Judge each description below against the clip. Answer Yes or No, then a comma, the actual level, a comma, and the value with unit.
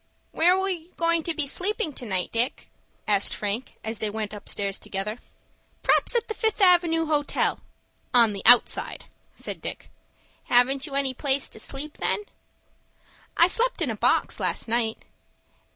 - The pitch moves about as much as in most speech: No, wide, 7.3 semitones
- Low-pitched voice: No, very high, 275 Hz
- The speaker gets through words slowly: No, average, 150 wpm